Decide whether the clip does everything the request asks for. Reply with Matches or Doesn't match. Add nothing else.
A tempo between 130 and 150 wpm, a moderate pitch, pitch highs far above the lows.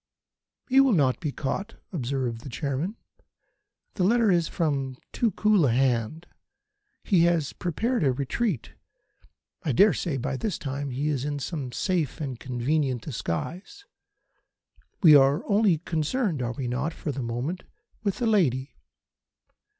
Matches